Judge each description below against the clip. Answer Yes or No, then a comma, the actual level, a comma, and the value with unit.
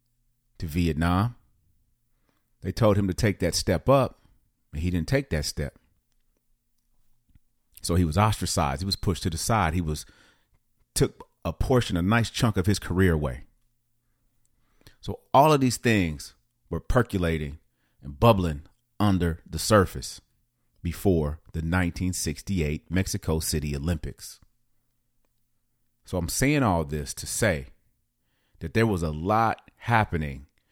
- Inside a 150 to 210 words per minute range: No, average, 140 wpm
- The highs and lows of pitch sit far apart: Yes, wide, 6.2 semitones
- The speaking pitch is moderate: No, very low, 95 Hz